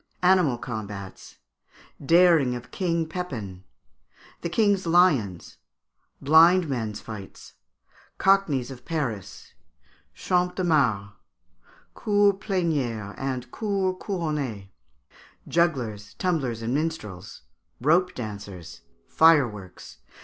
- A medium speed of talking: No, slow, 90 wpm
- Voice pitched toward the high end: No, medium, 140 Hz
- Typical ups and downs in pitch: No, wide, 8.4 semitones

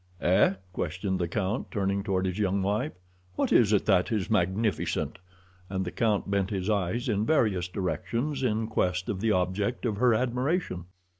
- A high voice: No, low, 100 Hz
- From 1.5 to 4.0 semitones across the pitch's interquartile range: Yes, average, 3.3 semitones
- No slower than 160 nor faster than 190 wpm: Yes, average, 170 wpm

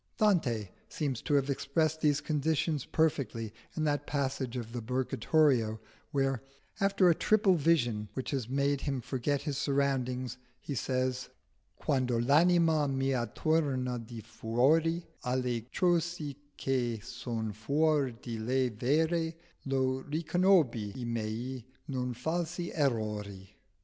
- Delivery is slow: Yes, slow, 125 wpm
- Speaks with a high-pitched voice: No, low, 135 Hz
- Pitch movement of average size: Yes, average, 4.5 semitones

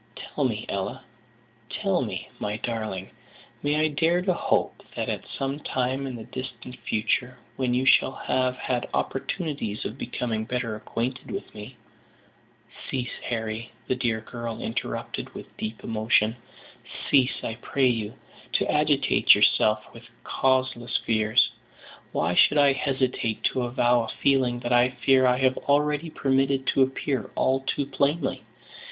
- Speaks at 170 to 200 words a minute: No, average, 150 wpm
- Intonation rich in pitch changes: No, average, 2.9 semitones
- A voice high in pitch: No, low, 125 Hz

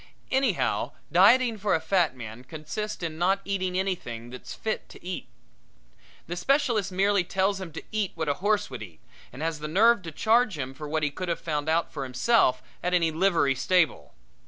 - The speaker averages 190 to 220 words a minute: Yes, average, 195 wpm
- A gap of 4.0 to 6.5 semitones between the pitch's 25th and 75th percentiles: Yes, average, 5.1 semitones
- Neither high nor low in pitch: Yes, medium, 175 Hz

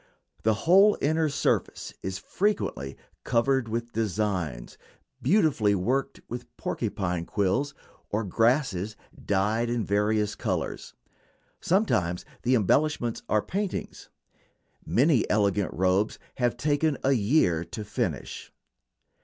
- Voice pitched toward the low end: Yes, low, 115 Hz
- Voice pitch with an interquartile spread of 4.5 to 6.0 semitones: Yes, wide, 5.5 semitones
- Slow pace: Yes, slow, 105 wpm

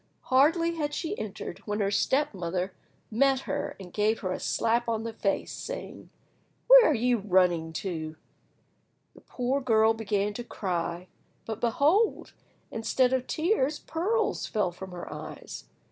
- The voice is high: Yes, high, 225 Hz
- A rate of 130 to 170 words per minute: Yes, average, 150 wpm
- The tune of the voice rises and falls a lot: Yes, wide, 6.4 semitones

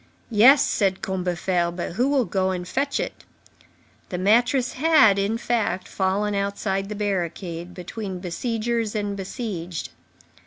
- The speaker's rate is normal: No, slow, 130 wpm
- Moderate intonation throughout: Yes, average, 3.7 semitones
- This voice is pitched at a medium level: No, high, 200 Hz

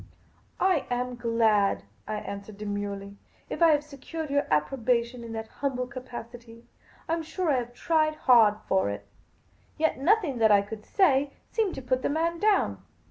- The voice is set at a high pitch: Yes, very high, 250 Hz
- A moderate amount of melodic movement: No, wide, 5.8 semitones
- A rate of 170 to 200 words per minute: Yes, average, 180 wpm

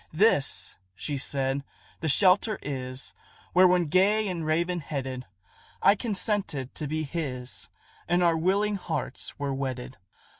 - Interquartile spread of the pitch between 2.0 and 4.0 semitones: No, wide, 5.4 semitones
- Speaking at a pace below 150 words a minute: Yes, slow, 135 wpm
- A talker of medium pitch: Yes, medium, 155 Hz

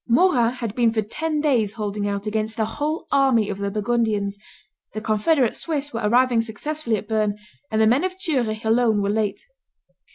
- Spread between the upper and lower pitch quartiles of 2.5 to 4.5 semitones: Yes, average, 3.5 semitones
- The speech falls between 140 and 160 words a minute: No, average, 185 wpm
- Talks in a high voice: Yes, high, 225 Hz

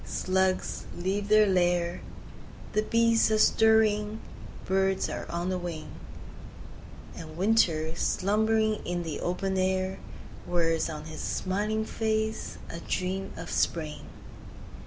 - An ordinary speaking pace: No, slow, 115 wpm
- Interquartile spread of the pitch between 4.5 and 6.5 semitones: No, average, 3.6 semitones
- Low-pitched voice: No, high, 190 Hz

